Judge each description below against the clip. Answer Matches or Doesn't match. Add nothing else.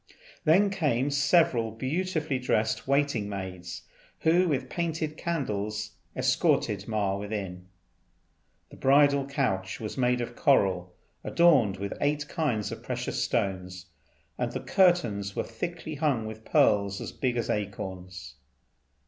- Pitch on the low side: Matches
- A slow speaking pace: Matches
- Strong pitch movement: Matches